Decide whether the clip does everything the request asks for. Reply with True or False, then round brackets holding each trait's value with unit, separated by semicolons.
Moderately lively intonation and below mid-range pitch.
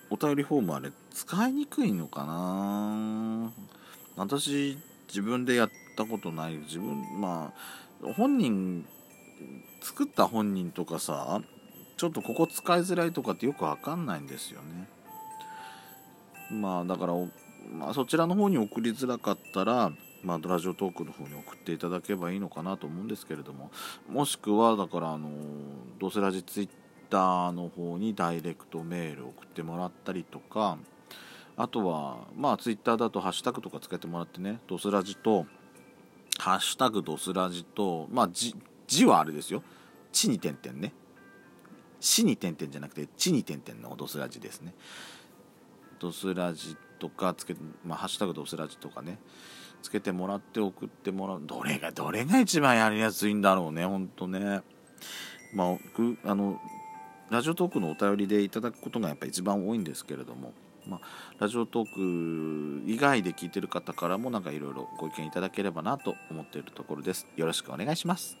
True (4.9 semitones; 100 Hz)